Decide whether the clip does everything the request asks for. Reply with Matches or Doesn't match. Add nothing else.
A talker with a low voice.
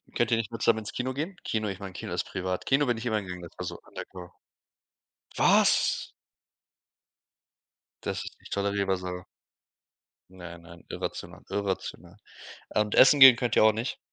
Matches